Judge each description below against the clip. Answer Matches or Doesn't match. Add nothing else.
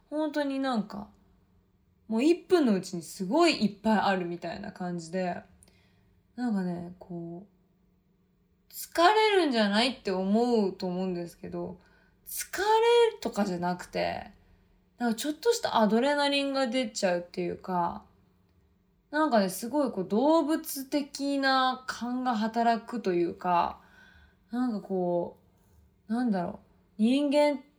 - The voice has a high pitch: Matches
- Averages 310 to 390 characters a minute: Doesn't match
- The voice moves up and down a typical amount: Doesn't match